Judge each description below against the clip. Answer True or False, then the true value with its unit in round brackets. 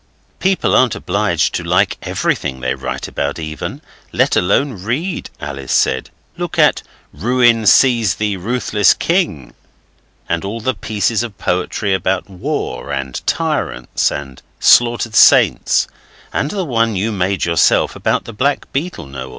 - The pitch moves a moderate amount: False (6.3 semitones)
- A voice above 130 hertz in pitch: False (105 Hz)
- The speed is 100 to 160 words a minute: True (140 wpm)